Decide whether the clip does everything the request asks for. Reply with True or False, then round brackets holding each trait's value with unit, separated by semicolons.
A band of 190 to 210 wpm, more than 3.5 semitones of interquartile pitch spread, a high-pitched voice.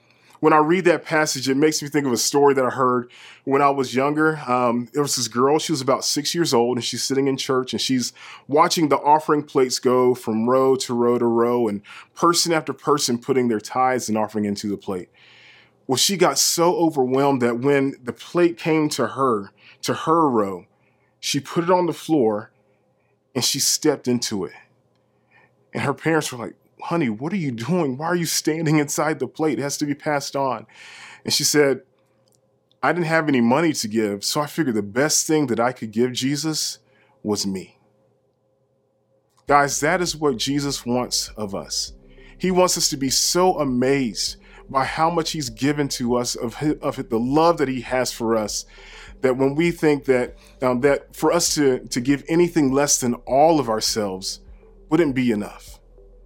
False (195 wpm; 4.1 semitones; 135 Hz)